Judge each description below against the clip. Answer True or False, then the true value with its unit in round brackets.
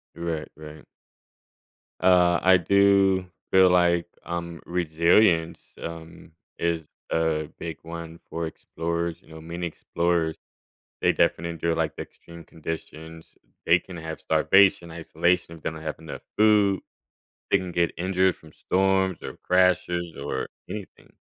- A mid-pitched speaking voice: False (85 Hz)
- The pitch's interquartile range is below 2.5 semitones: True (2.0 semitones)